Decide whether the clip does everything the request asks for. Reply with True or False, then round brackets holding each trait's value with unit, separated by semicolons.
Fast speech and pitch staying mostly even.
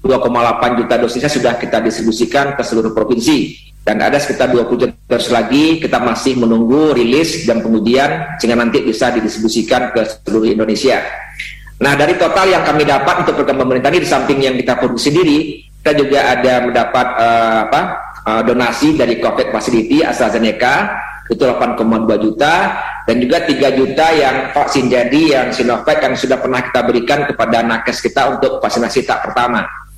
False (160 wpm; 3.7 semitones)